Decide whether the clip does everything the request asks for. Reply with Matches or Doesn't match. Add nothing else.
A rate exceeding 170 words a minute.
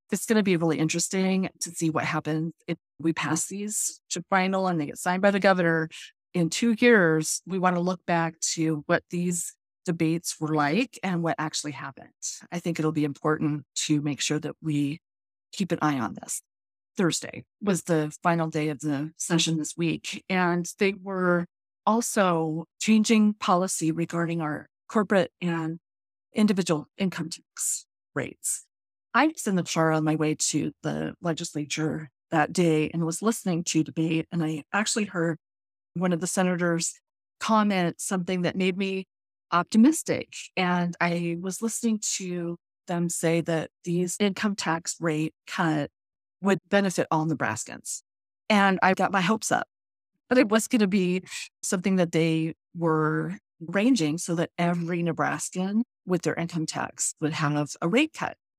Doesn't match